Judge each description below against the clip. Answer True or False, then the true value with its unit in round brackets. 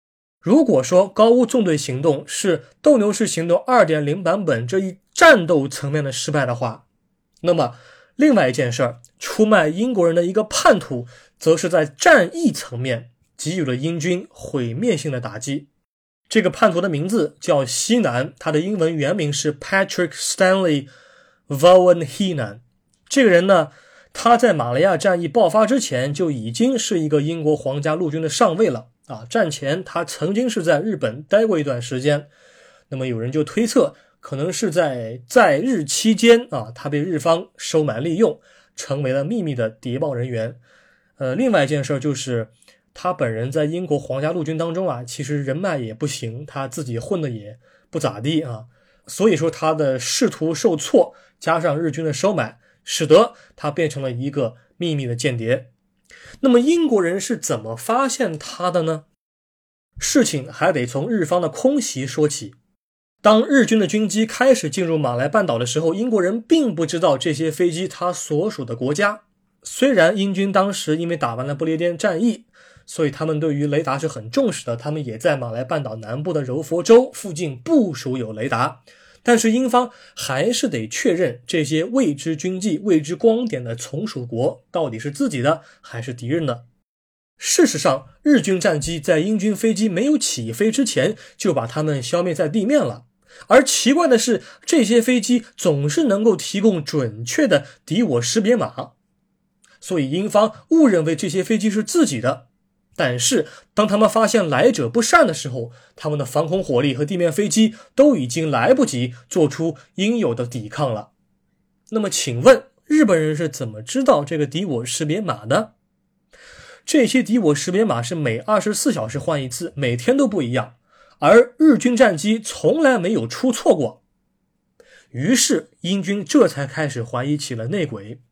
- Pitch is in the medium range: True (165 Hz)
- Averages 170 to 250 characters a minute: False (270 characters per minute)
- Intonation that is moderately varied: False (7.7 semitones)